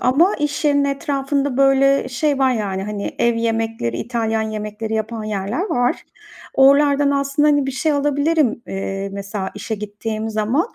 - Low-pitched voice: No, high, 245 Hz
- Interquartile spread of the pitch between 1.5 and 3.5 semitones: No, average, 4.7 semitones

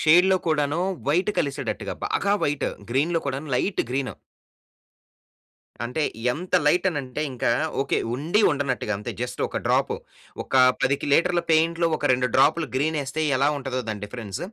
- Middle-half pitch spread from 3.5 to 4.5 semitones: Yes, average, 4.1 semitones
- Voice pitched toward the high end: No, medium, 145 Hz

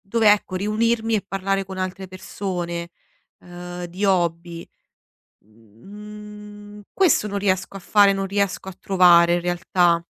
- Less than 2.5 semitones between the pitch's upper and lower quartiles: No, average, 2.8 semitones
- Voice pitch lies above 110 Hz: Yes, high, 190 Hz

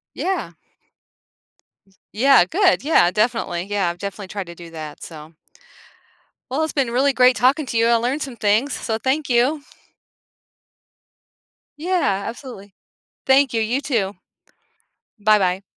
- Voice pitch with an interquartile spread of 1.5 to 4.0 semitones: No, wide, 5.6 semitones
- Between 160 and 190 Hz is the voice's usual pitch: No, high, 235 Hz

